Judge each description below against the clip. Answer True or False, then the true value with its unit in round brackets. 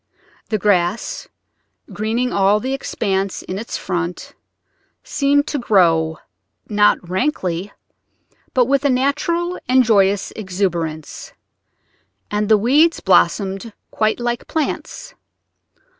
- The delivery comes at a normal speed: False (105 wpm)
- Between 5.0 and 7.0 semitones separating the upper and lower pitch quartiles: True (5.4 semitones)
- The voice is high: True (210 Hz)